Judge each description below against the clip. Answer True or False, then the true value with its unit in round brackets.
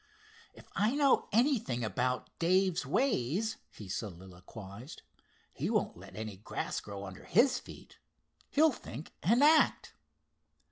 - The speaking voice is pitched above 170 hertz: False (135 Hz)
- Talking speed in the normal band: False (125 wpm)